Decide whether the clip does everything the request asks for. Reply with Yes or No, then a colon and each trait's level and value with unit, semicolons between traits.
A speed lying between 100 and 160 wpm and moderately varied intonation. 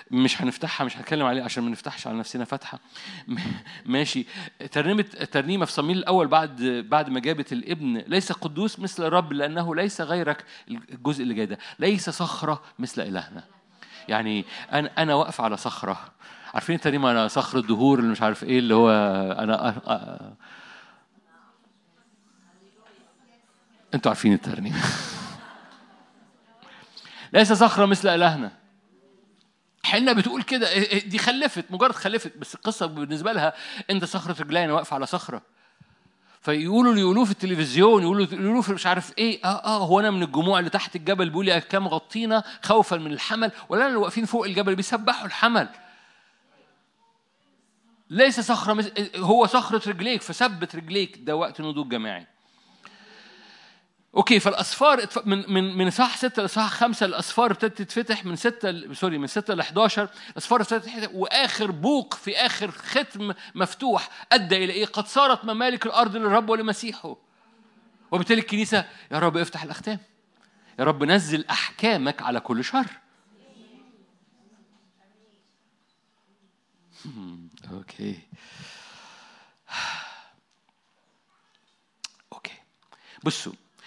Yes: average, 125 wpm; average, 5.0 semitones